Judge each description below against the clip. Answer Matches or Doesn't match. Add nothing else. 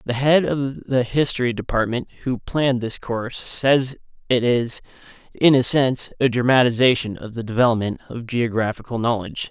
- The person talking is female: Doesn't match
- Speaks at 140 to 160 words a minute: Matches